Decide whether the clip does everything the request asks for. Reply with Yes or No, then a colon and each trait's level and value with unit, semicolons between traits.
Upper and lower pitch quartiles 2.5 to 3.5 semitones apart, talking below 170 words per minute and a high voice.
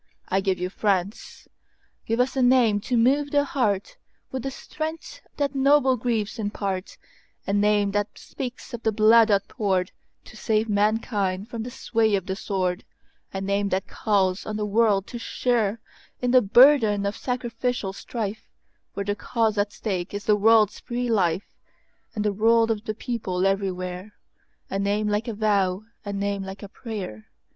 Yes: average, 3.1 semitones; average, 150 wpm; high, 210 Hz